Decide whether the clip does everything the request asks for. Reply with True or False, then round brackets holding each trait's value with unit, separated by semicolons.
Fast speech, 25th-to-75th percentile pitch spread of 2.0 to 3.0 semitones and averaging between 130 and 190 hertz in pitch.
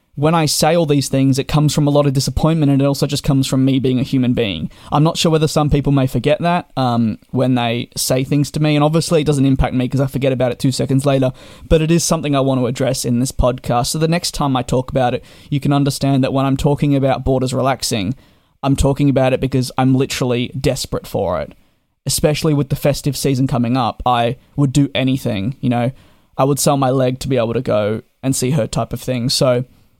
True (245 wpm; 2.4 semitones; 135 Hz)